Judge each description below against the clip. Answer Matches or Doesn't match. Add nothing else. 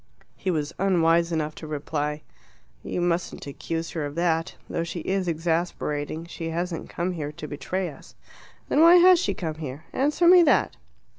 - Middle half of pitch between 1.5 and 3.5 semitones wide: Matches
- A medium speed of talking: Matches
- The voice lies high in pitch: Doesn't match